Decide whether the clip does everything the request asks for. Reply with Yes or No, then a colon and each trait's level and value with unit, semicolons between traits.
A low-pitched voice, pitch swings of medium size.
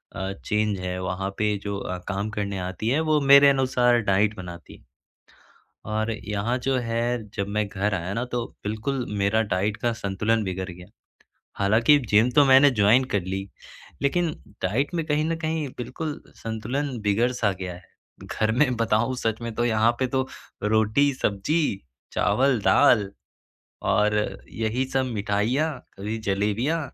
Yes: low, 110 Hz; average, 4.3 semitones